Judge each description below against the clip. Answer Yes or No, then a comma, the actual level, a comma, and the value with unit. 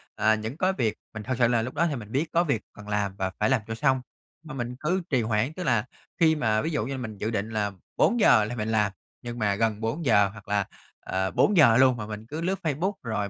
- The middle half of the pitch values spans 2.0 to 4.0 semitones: No, average, 4.7 semitones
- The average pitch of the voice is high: No, low, 115 Hz